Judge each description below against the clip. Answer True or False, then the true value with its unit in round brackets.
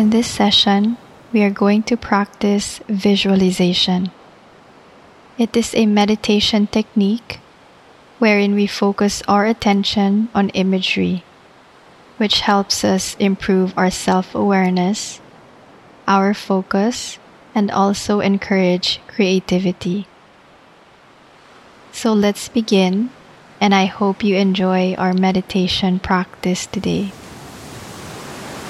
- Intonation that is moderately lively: False (1.9 semitones)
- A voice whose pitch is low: False (200 Hz)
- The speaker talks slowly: True (95 wpm)